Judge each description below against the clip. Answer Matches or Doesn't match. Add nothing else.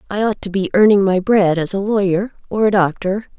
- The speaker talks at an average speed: Doesn't match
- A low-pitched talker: Doesn't match